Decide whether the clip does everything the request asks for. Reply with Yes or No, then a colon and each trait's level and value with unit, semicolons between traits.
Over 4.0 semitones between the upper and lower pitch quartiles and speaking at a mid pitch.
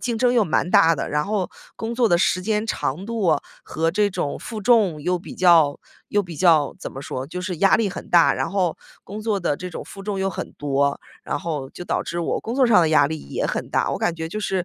Yes: average, 4.5 semitones; medium, 180 Hz